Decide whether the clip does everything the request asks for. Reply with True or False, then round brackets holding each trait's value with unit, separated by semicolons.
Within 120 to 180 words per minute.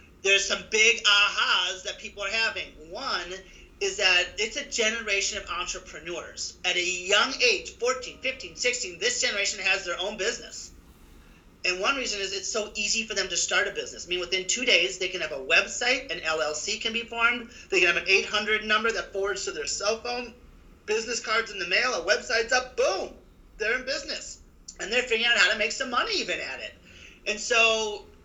False (200 wpm)